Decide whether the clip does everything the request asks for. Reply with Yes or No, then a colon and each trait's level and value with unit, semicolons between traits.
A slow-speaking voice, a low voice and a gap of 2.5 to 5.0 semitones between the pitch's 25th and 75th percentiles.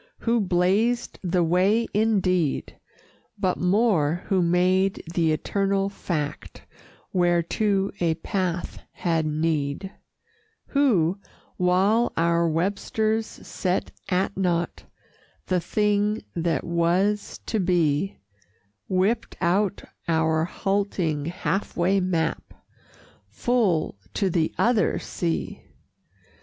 No: slow, 95 wpm; medium, 180 Hz; average, 3.1 semitones